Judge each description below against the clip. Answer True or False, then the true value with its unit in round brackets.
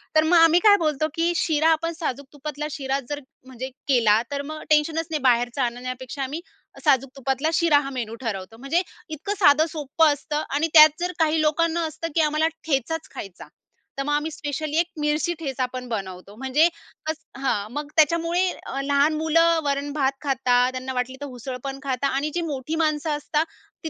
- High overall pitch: True (290 Hz)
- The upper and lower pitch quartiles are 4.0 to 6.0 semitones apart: False (3.3 semitones)